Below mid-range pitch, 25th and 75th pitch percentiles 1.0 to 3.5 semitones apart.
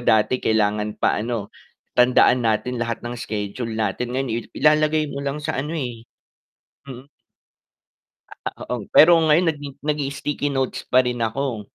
No: low, 125 Hz; average, 4.1 semitones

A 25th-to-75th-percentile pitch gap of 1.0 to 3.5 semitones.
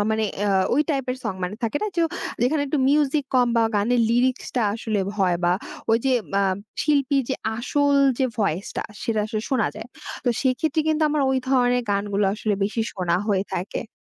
No: average, 4.8 semitones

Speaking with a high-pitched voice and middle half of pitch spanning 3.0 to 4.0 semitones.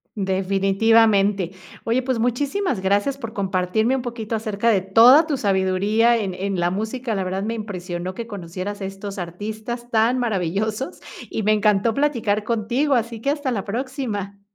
Yes: high, 215 Hz; average, 3.4 semitones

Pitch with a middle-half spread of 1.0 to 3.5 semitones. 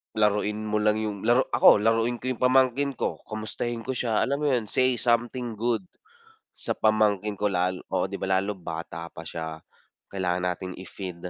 No: average, 4.2 semitones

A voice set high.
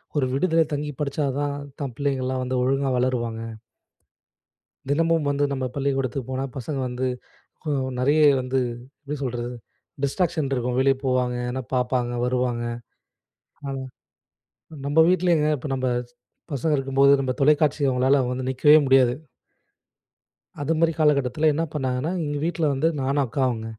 No: low, 135 Hz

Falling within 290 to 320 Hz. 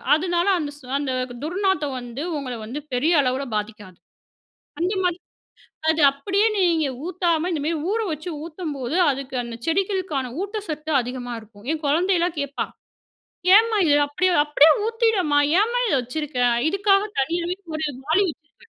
Yes: very high, 315 Hz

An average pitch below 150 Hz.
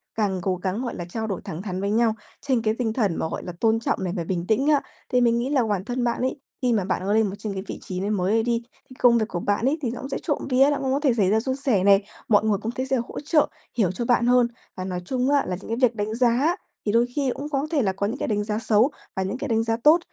No: high, 225 Hz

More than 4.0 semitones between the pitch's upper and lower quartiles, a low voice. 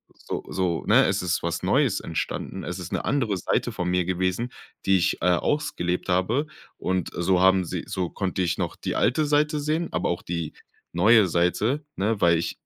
Yes: average, 5.0 semitones; very low, 95 Hz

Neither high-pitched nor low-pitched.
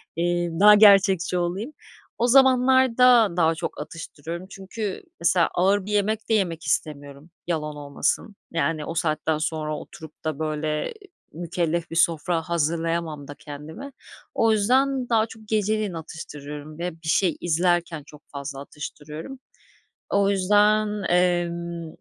Yes: medium, 170 Hz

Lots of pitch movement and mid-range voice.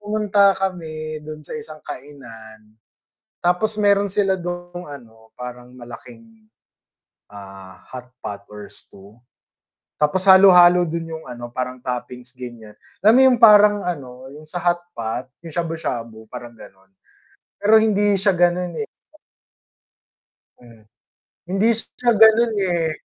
Yes: wide, 8.0 semitones; medium, 160 Hz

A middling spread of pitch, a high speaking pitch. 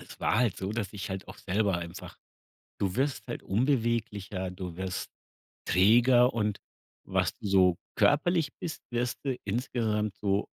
No: average, 4.3 semitones; low, 105 Hz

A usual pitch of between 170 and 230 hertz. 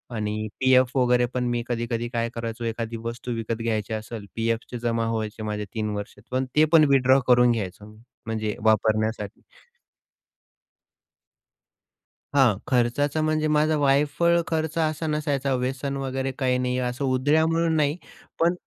No: low, 125 Hz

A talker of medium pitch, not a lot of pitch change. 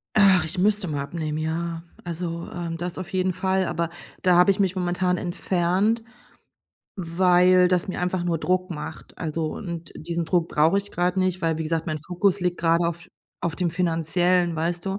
Yes: medium, 175 Hz; narrow, 1.8 semitones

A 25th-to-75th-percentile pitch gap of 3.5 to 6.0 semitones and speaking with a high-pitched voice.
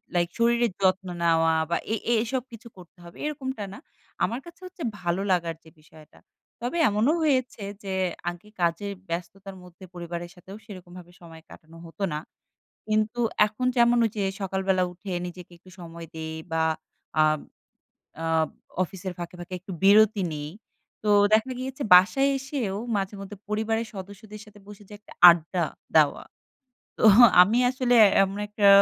Yes: average, 4.2 semitones; high, 195 Hz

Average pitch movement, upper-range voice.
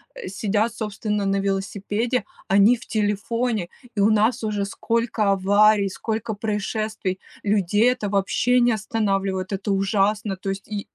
No: narrow, 2.0 semitones; high, 210 Hz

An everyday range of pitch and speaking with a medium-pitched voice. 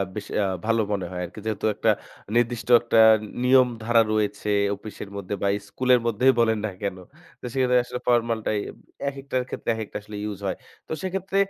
No: average, 3.2 semitones; low, 115 Hz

